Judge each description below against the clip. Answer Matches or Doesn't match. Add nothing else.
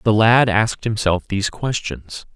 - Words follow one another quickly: Doesn't match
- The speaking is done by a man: Matches